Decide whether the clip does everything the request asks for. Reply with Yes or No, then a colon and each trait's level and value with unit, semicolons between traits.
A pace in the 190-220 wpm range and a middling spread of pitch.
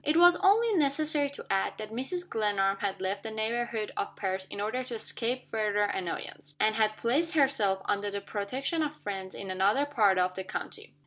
No: average, 195 wpm; wide, 5.8 semitones